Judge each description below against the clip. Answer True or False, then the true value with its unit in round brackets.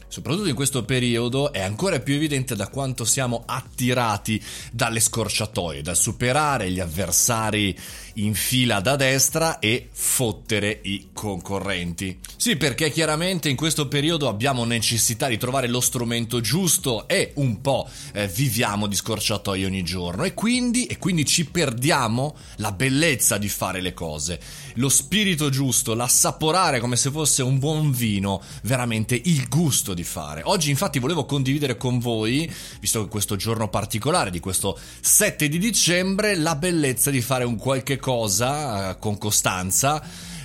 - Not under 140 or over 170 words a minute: True (150 wpm)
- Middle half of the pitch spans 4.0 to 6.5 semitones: True (5.5 semitones)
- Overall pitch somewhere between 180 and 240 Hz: False (125 Hz)